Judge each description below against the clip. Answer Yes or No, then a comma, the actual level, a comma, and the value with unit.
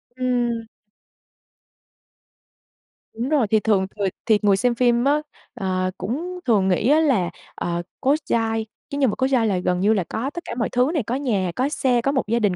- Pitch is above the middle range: Yes, high, 235 Hz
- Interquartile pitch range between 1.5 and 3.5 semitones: No, average, 4.4 semitones